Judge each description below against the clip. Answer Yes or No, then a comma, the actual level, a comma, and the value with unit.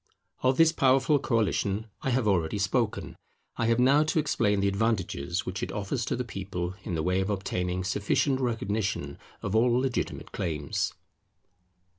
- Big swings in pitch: No, average, 5.0 semitones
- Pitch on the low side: Yes, low, 105 Hz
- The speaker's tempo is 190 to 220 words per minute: No, average, 160 wpm